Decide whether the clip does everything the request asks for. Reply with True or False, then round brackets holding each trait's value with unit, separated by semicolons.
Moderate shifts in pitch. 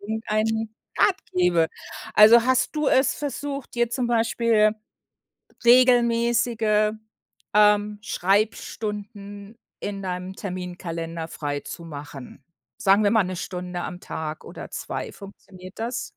True (4.2 semitones)